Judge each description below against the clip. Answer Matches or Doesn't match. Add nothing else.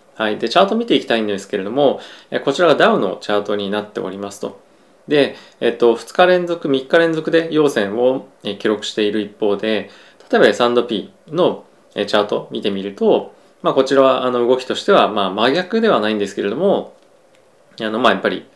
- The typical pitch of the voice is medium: Doesn't match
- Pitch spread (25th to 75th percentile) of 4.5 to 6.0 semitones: Doesn't match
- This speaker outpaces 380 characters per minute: Doesn't match